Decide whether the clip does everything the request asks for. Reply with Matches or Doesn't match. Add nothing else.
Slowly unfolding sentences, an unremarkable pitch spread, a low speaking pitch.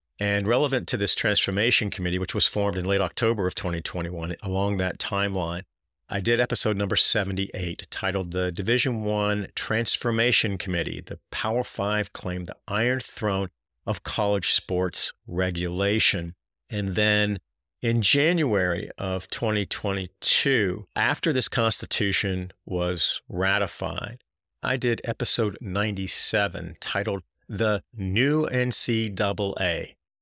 Matches